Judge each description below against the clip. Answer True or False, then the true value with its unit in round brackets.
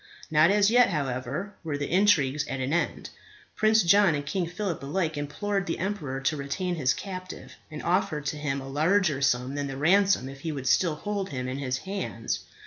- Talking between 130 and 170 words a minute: False (200 wpm)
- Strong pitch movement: True (5.7 semitones)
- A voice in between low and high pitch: True (155 Hz)